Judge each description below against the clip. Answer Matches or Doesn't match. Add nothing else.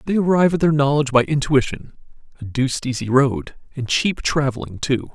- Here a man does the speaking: Matches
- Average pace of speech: Matches